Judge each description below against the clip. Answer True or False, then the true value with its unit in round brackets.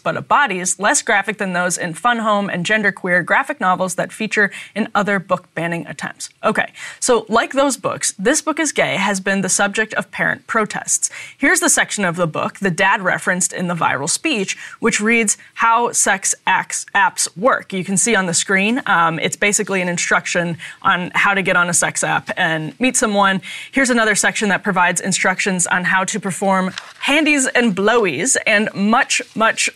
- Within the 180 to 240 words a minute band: True (190 wpm)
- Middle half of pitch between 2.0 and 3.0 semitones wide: False (3.8 semitones)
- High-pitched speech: True (200 Hz)